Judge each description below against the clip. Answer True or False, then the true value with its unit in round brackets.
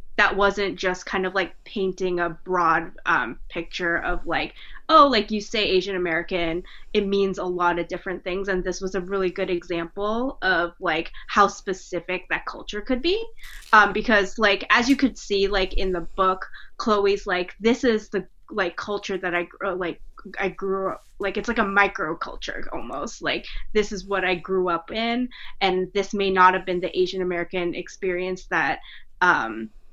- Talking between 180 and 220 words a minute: True (185 wpm)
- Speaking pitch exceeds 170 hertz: True (190 Hz)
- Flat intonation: True (2.2 semitones)